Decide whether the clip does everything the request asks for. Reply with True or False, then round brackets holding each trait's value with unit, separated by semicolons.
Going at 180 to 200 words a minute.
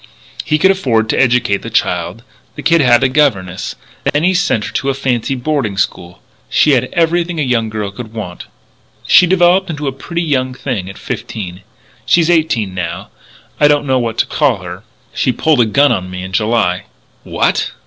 True (195 wpm)